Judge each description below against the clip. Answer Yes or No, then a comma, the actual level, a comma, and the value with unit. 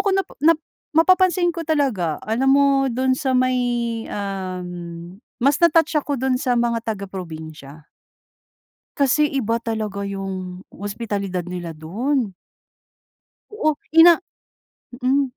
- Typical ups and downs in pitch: No, wide, 6.5 semitones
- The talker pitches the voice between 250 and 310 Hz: No, high, 235 Hz